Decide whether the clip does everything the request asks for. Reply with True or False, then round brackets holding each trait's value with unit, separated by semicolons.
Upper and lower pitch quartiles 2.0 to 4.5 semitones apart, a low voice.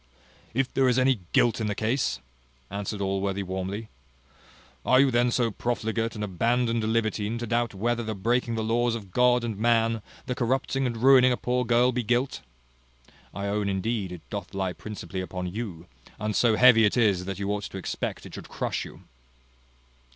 True (3.3 semitones; 115 Hz)